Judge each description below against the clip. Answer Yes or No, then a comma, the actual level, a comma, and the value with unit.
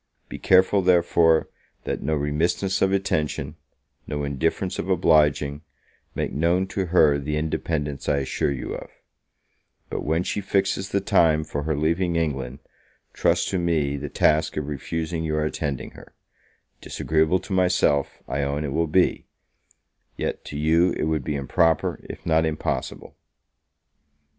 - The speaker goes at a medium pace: Yes, average, 150 wpm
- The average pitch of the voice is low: Yes, very low, 80 Hz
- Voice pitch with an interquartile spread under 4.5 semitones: Yes, average, 3.0 semitones